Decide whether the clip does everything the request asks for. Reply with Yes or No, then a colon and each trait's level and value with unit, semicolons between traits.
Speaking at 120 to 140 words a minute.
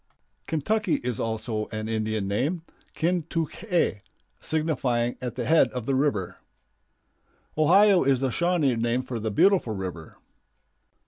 Yes: slow, 135 wpm